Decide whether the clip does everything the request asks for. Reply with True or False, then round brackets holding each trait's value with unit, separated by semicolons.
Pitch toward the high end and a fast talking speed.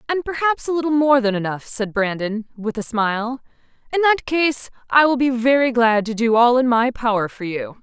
True (245 Hz; 215 wpm)